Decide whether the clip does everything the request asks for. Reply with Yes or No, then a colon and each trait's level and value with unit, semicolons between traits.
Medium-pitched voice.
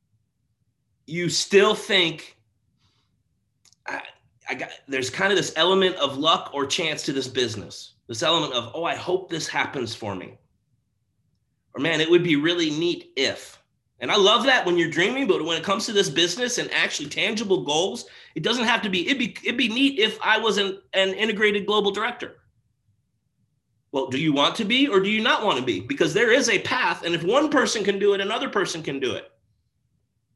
Yes: medium, 170 Hz